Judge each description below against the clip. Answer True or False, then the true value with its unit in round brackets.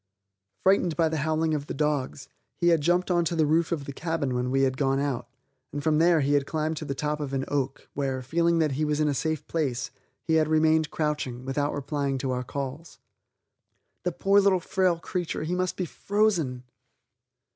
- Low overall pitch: False (150 Hz)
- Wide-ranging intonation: False (3.3 semitones)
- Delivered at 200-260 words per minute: True (205 wpm)